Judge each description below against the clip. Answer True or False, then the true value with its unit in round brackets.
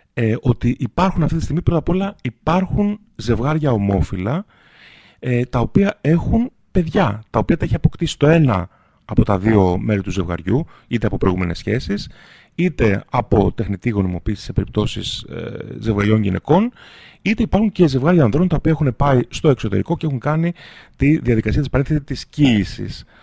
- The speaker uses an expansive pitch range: True (7.1 semitones)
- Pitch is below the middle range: True (125 Hz)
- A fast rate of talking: False (160 wpm)